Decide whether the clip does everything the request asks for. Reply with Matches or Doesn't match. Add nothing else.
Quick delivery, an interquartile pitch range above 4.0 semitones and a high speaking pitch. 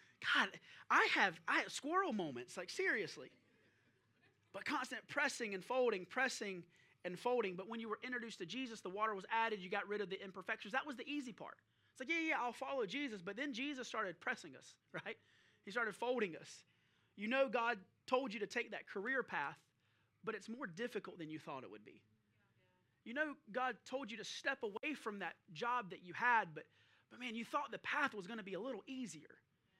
Matches